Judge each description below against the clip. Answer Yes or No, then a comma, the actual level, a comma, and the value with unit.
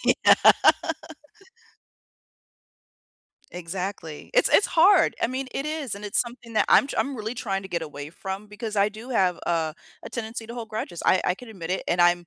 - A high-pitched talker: Yes, high, 210 Hz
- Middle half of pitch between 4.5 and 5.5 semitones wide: Yes, average, 5.1 semitones